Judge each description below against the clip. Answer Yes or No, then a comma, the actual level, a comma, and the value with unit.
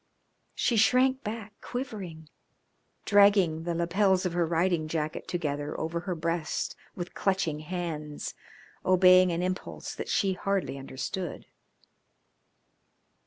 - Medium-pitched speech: Yes, medium, 175 Hz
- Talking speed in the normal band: No, slow, 115 wpm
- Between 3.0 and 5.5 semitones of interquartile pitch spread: Yes, average, 3.4 semitones